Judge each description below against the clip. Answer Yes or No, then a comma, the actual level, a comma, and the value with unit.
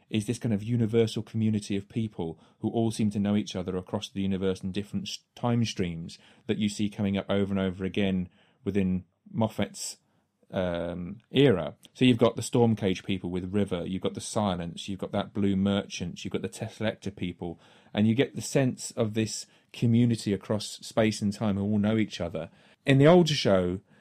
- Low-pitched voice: Yes, low, 105 Hz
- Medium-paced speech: Yes, average, 195 wpm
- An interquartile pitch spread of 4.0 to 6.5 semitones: No, average, 2.8 semitones